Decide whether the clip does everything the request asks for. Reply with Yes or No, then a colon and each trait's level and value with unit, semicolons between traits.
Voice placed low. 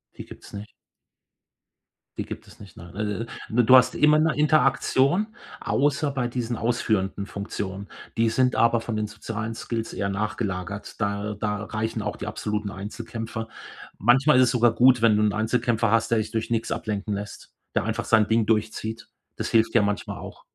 Yes: low, 110 Hz